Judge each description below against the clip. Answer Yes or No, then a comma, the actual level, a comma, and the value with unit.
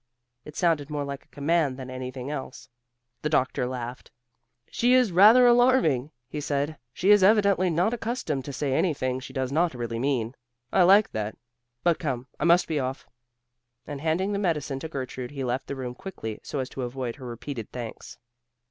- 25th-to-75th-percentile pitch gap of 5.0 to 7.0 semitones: Yes, average, 5.3 semitones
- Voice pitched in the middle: Yes, medium, 145 Hz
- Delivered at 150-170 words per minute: No, average, 185 wpm